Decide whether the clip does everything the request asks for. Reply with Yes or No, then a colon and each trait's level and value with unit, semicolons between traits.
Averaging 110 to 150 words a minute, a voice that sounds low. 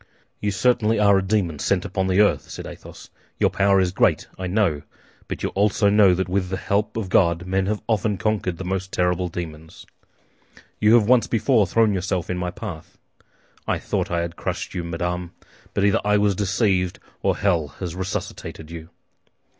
No: average, 185 wpm; very low, 95 Hz